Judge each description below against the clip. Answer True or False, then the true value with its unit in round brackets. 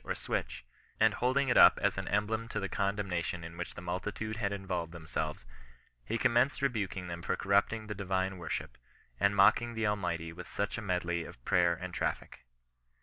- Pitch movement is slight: False (3.8 semitones)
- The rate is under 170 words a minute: False (195 wpm)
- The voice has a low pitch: True (95 Hz)